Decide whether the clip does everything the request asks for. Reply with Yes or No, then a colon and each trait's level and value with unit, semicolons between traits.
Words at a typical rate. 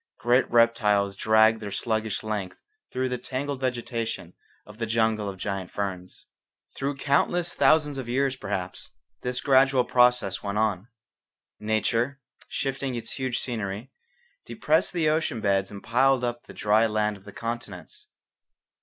Yes: average, 145 wpm